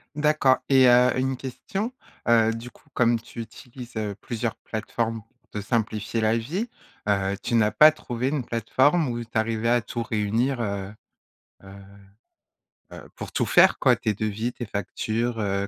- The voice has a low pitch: Yes, low, 115 Hz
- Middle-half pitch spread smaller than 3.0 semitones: Yes, narrow, 2.6 semitones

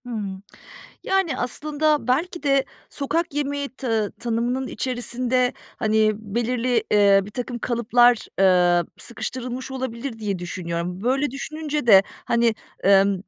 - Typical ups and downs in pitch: Yes, average, 4.2 semitones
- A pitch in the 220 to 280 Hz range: Yes, high, 240 Hz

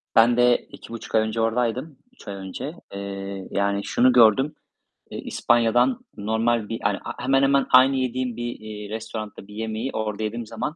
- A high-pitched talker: No, low, 115 Hz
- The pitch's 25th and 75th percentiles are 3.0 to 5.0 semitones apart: No, narrow, 2.6 semitones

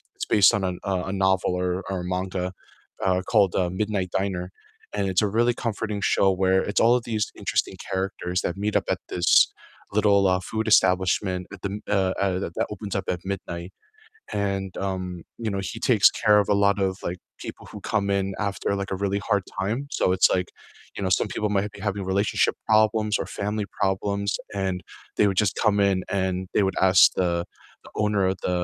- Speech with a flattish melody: Yes, narrow, 1.9 semitones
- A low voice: Yes, low, 100 Hz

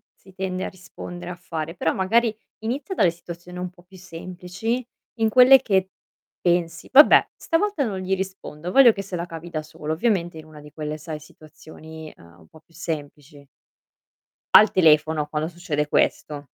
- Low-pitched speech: No, medium, 175 Hz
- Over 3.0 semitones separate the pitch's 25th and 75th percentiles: Yes, average, 3.5 semitones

